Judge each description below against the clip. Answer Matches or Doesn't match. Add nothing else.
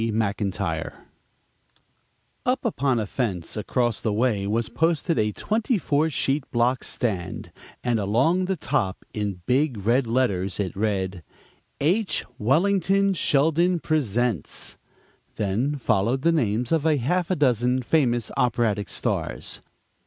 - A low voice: Matches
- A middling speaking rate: Doesn't match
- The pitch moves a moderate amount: Doesn't match